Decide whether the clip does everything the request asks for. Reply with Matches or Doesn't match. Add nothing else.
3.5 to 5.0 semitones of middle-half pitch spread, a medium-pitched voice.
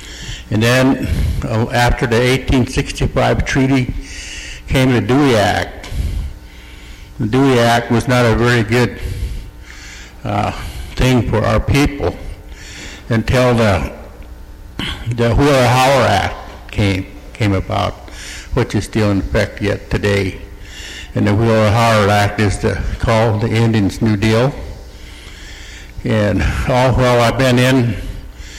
Doesn't match